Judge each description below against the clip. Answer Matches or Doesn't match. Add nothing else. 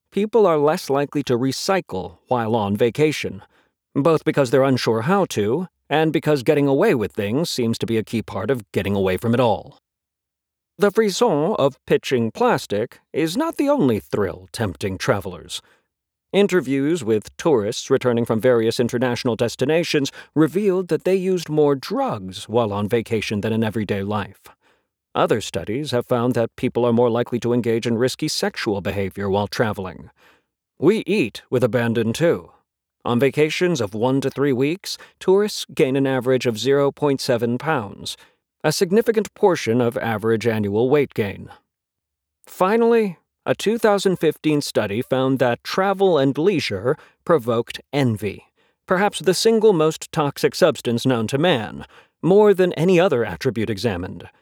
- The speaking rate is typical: Matches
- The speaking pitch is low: Matches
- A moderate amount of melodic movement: Doesn't match